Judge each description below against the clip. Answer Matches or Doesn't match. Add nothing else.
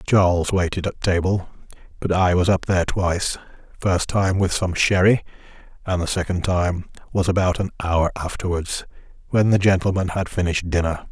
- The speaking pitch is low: Matches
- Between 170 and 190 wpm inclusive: Doesn't match